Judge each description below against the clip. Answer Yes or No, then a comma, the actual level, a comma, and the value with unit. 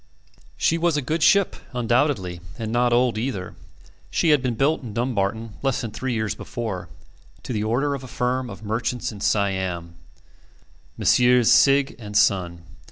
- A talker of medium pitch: No, low, 120 Hz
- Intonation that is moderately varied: Yes, average, 4.2 semitones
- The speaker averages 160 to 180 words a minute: Yes, average, 165 wpm